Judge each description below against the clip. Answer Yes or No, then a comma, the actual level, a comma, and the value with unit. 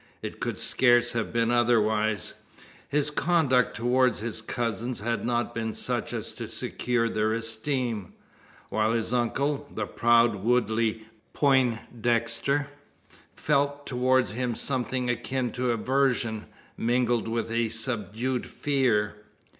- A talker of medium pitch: No, low, 120 Hz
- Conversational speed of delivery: No, slow, 120 wpm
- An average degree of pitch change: No, narrow, 2.3 semitones